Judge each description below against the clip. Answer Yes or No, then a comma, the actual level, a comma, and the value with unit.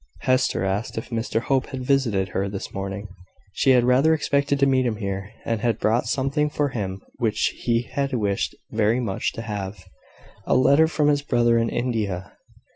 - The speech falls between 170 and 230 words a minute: Yes, average, 185 wpm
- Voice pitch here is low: Yes, low, 120 Hz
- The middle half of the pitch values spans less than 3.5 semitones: No, average, 4.6 semitones